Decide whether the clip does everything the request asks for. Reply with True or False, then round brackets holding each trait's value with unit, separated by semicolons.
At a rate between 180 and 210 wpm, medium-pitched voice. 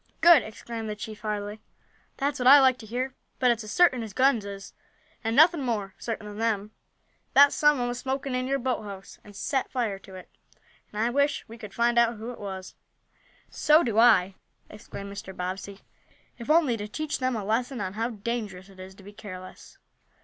False (200 wpm; 225 Hz)